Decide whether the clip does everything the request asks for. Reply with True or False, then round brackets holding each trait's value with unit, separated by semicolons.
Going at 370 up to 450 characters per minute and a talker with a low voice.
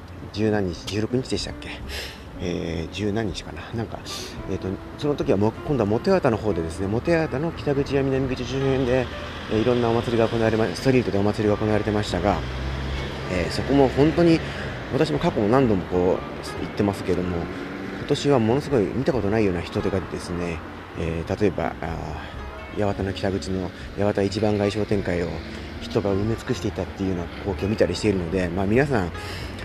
True (385 characters per minute; 100 Hz)